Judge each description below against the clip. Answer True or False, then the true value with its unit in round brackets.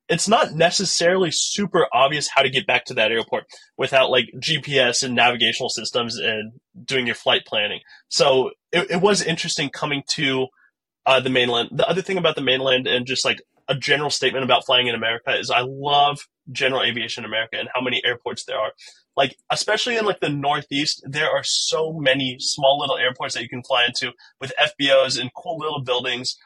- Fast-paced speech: False (195 wpm)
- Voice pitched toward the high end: False (135 Hz)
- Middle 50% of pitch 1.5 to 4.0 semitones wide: False (4.8 semitones)